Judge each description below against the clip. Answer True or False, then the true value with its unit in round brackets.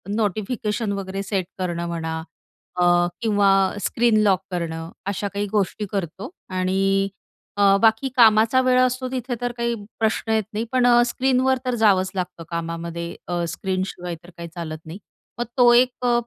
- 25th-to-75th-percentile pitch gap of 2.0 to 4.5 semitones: False (5.1 semitones)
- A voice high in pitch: True (200 Hz)